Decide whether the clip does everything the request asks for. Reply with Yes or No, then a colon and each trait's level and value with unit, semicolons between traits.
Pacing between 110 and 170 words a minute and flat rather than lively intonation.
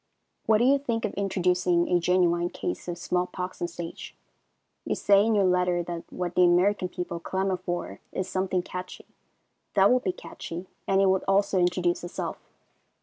No: average, 185 wpm; narrow, 1.7 semitones